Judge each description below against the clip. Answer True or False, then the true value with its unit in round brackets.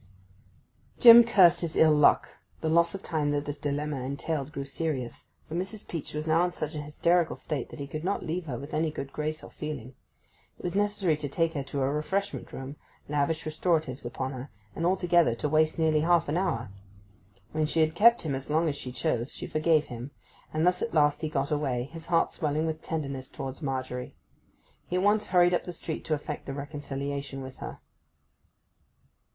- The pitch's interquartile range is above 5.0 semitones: False (3.1 semitones)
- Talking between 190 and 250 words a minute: True (200 wpm)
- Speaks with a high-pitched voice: False (155 Hz)